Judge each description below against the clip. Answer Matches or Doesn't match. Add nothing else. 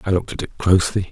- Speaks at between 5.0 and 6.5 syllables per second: Doesn't match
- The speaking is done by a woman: Doesn't match